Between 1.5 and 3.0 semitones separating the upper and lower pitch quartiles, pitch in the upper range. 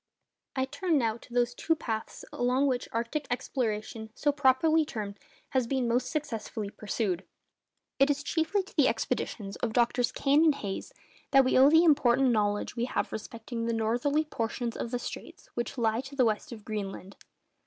No: average, 3.7 semitones; high, 245 Hz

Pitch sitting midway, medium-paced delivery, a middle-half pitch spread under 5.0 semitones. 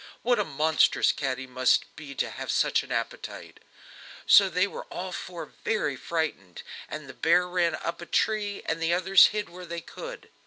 Yes: medium, 170 Hz; average, 190 wpm; average, 3.6 semitones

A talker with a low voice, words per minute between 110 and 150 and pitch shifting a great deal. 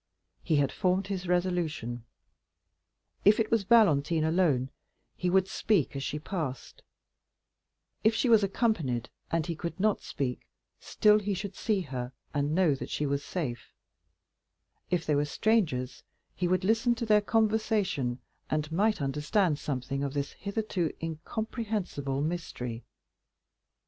No: medium, 170 Hz; average, 140 wpm; wide, 6.4 semitones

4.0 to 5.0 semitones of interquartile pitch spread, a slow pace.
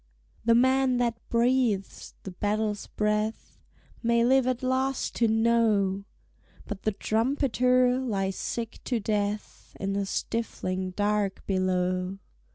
No: average, 3.6 semitones; slow, 120 wpm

